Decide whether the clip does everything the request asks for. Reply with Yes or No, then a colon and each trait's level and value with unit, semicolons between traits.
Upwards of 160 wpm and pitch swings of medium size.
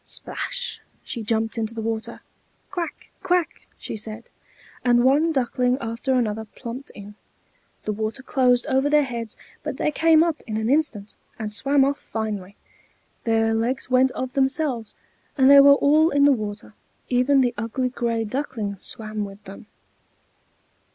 No: average, 155 wpm; average, 4.1 semitones